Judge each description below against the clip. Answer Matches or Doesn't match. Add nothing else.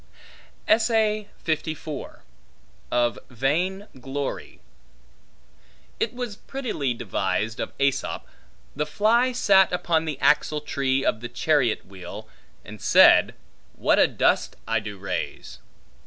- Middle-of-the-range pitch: Matches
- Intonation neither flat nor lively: Doesn't match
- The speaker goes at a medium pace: Doesn't match